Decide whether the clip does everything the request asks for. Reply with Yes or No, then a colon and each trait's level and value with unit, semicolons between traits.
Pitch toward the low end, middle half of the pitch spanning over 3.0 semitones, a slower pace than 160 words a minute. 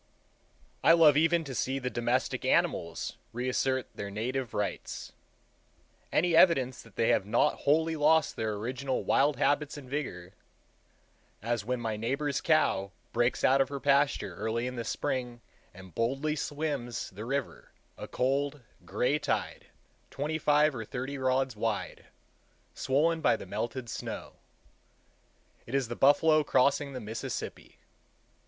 Yes: low, 130 Hz; average, 3.9 semitones; average, 140 wpm